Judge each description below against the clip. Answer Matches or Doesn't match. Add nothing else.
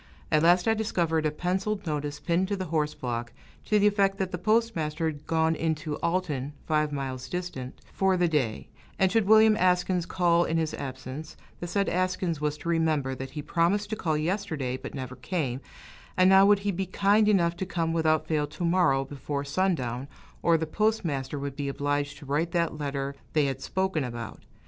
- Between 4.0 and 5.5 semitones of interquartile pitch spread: Matches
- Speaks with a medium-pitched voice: Matches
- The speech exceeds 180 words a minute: Matches